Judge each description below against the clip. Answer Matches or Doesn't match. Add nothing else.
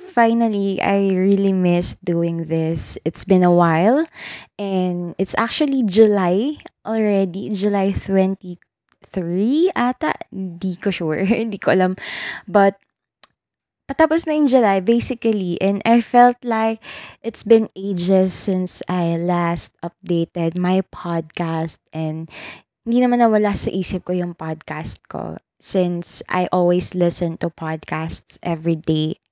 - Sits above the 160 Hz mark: Matches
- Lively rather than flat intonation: Doesn't match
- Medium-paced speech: Matches